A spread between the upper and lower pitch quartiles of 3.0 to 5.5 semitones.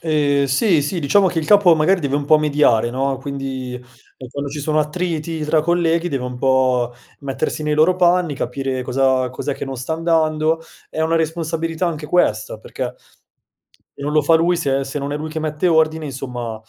Yes: average, 3.4 semitones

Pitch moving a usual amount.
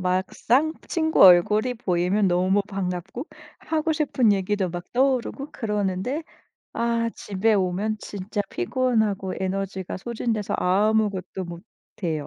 Yes: average, 4.0 semitones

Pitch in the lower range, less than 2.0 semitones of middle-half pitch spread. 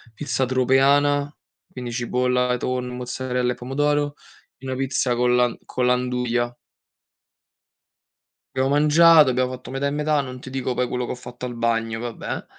Yes: low, 125 Hz; narrow, 1.6 semitones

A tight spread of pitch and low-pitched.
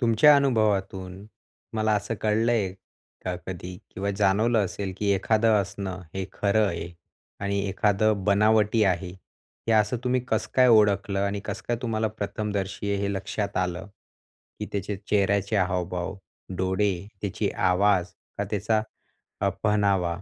Yes: narrow, 2.1 semitones; low, 100 Hz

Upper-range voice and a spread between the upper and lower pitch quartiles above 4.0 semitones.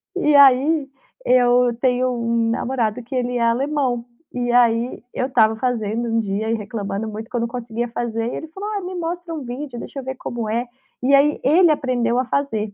No: high, 245 Hz; average, 3.0 semitones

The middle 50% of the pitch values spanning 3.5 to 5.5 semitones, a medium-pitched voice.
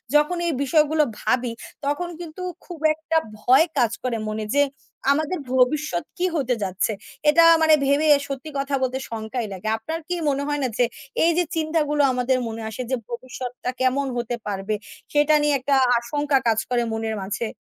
No: average, 4.3 semitones; very high, 270 Hz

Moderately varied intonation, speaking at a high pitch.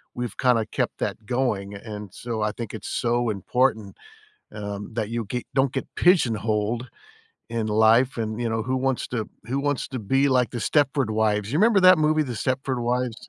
No: average, 3.3 semitones; low, 120 Hz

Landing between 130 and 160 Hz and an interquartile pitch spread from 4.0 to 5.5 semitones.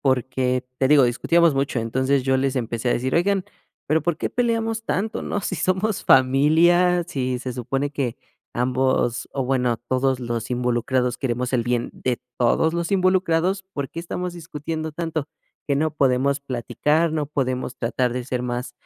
Yes: low, 135 Hz; average, 4.6 semitones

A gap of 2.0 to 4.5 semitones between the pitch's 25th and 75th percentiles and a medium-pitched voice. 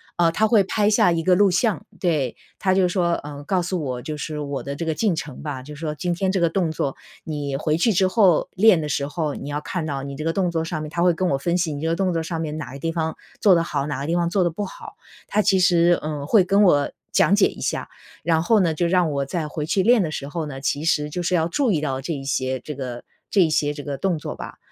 Yes: average, 3.6 semitones; medium, 165 Hz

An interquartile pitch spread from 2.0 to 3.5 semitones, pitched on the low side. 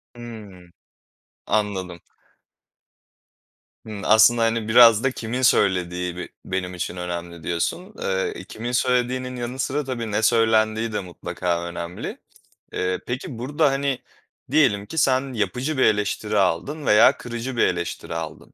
No: wide, 5.5 semitones; low, 110 Hz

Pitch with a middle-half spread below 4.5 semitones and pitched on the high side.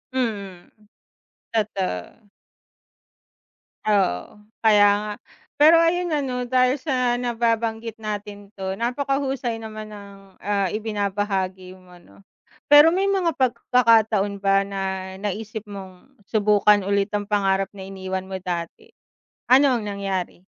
Yes: average, 4.0 semitones; high, 210 Hz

